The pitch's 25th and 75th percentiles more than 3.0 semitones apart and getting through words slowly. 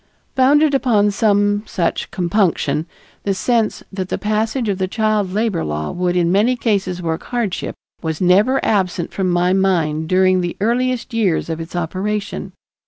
No: average, 3.7 semitones; average, 160 wpm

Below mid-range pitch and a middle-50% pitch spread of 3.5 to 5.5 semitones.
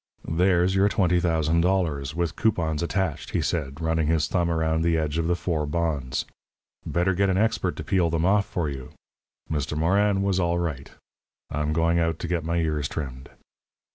No: very low, 85 Hz; narrow, 2.4 semitones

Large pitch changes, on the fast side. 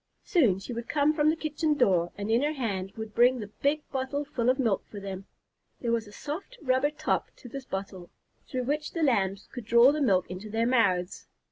Yes: wide, 6.1 semitones; fast, 220 wpm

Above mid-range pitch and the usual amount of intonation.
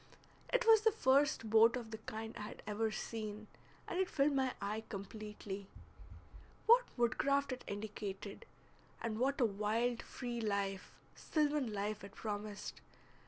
Yes: high, 220 Hz; average, 4.3 semitones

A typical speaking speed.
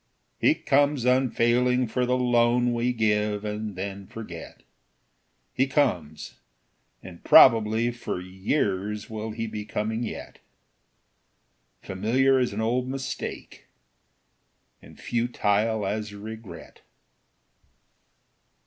No: slow, 100 wpm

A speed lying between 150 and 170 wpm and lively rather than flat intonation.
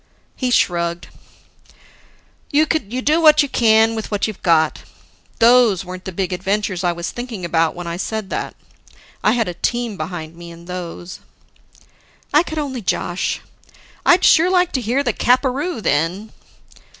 Yes: average, 160 wpm; wide, 6.3 semitones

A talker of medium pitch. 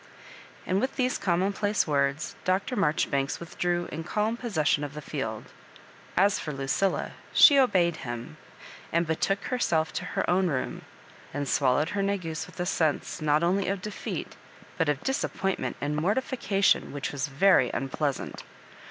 Yes: medium, 170 Hz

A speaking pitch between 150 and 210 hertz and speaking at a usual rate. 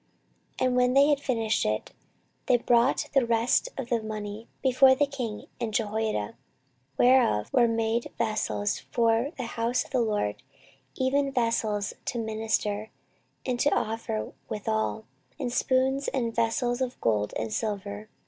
No: high, 230 Hz; average, 150 wpm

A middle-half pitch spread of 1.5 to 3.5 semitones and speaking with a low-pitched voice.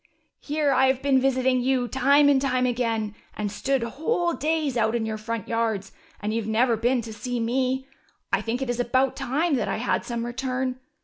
No: narrow, 2.6 semitones; very high, 255 Hz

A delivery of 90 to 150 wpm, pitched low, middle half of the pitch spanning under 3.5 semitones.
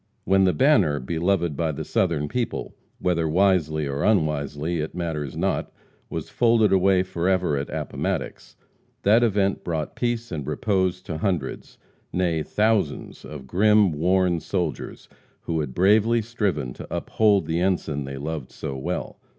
No: average, 145 wpm; very low, 90 Hz; average, 4.4 semitones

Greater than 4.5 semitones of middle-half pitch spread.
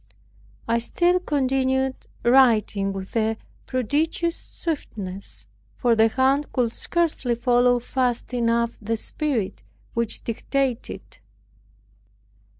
No: average, 3.0 semitones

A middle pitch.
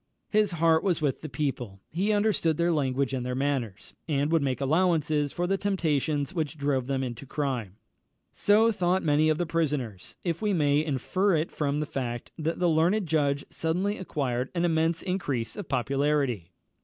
Yes: medium, 150 Hz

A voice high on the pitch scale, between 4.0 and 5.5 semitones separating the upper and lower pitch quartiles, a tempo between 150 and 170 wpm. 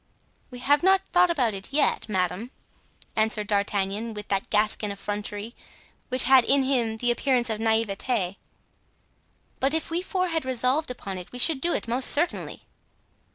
Yes: high, 240 Hz; average, 4.9 semitones; average, 160 wpm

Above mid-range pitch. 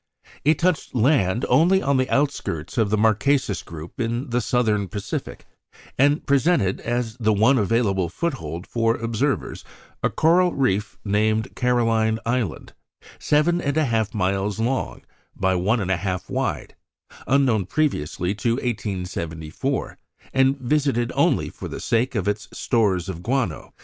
No: low, 115 Hz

